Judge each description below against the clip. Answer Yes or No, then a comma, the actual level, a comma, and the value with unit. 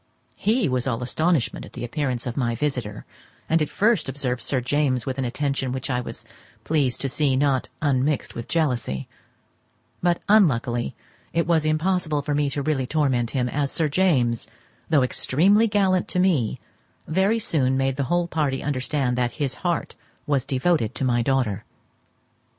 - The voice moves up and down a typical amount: Yes, average, 4.2 semitones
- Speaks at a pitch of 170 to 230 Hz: No, medium, 140 Hz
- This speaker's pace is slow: No, average, 165 wpm